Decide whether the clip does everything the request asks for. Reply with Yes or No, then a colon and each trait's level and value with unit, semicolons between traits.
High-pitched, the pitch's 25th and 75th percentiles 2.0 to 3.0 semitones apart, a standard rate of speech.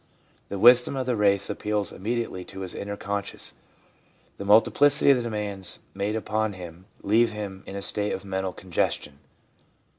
No: low, 100 Hz; narrow, 2.6 semitones; average, 160 wpm